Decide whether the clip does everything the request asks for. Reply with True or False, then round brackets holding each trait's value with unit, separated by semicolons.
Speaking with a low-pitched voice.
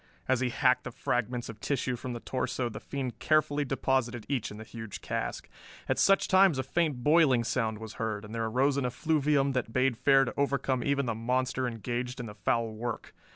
True (125 Hz)